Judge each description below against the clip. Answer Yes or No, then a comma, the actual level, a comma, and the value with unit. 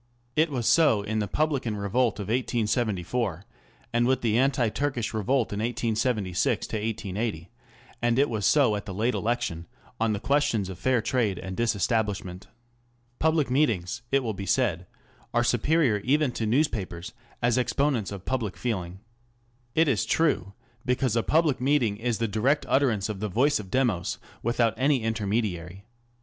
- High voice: No, low, 115 Hz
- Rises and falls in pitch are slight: No, average, 4.1 semitones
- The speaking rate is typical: Yes, average, 160 wpm